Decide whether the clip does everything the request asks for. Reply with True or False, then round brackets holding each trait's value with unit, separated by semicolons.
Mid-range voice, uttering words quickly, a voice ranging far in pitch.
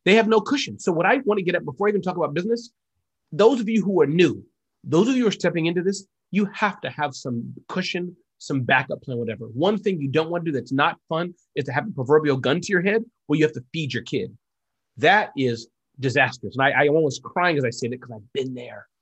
True (160 Hz; 260 wpm; 6.8 semitones)